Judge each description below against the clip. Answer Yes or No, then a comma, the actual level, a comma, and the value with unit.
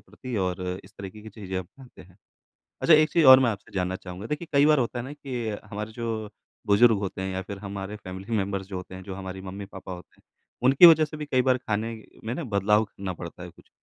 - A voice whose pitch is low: Yes, low, 105 Hz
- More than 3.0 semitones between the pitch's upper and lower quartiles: Yes, average, 4.7 semitones